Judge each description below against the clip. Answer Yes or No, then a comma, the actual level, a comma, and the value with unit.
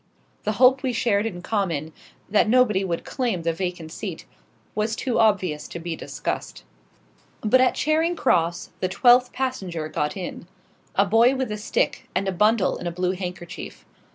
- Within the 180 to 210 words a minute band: No, average, 170 wpm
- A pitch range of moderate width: No, wide, 5.7 semitones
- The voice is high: Yes, high, 200 Hz